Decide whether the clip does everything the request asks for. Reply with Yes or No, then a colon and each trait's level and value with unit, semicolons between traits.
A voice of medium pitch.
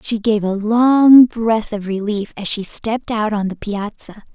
No: high, 215 Hz